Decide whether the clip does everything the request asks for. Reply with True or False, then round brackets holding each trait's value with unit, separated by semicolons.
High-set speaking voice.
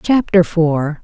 False (170 Hz)